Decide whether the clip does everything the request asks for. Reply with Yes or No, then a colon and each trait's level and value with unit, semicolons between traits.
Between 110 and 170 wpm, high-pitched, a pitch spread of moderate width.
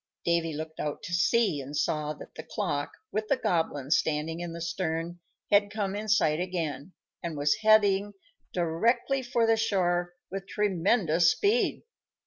No: average, 155 wpm; medium, 175 Hz; average, 4.6 semitones